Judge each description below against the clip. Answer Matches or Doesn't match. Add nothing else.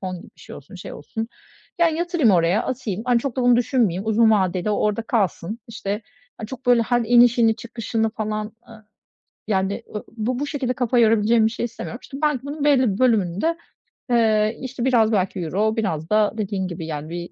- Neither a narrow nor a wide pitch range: Matches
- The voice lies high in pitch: Matches